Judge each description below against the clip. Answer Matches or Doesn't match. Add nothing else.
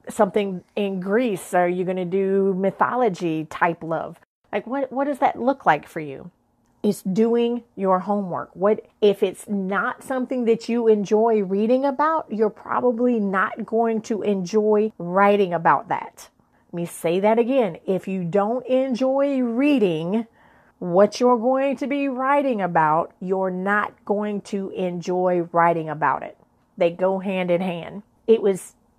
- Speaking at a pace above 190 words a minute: Doesn't match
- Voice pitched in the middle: Doesn't match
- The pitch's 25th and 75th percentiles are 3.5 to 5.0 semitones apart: Matches